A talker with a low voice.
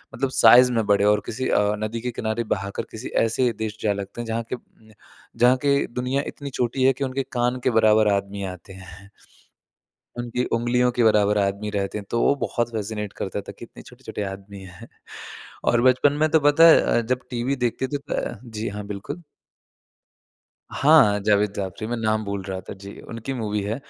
Yes: low, 110 Hz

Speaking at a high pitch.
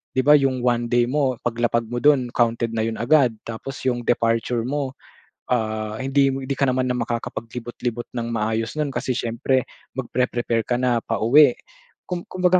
No: low, 120 Hz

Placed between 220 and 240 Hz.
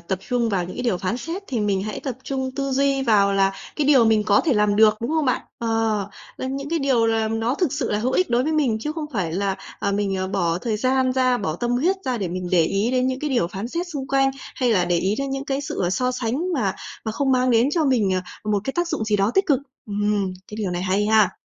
Yes: high, 230 Hz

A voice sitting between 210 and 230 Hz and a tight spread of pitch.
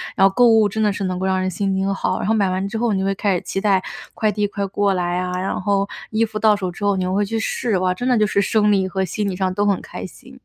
No: high, 195 Hz; narrow, 2.0 semitones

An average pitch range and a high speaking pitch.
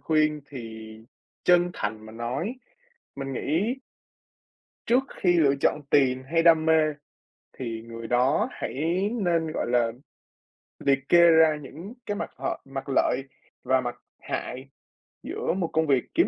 No: average, 4.7 semitones; medium, 150 Hz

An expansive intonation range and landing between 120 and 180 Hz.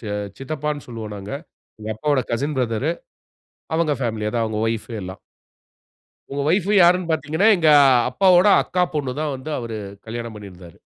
Yes: wide, 6.1 semitones; low, 135 Hz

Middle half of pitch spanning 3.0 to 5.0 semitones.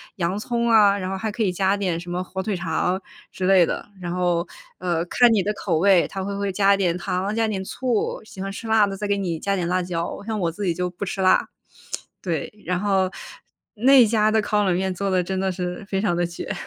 No: narrow, 2.4 semitones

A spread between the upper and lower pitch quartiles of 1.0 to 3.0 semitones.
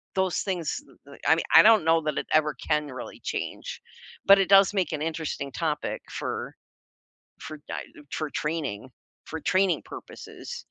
No: average, 3.7 semitones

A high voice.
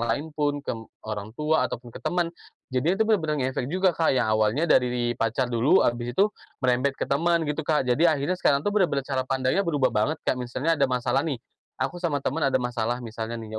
No: low, 135 Hz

